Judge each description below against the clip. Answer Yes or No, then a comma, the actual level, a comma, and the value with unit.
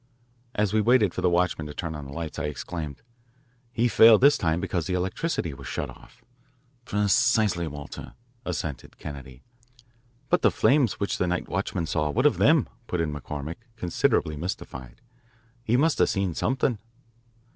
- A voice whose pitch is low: Yes, very low, 90 Hz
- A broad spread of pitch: Yes, wide, 6.4 semitones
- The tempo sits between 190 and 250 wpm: No, average, 165 wpm